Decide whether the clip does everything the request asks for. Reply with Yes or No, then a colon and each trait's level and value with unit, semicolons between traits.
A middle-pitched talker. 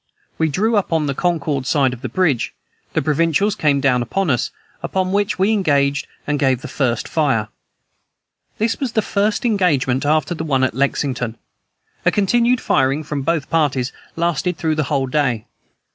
Yes: medium, 150 Hz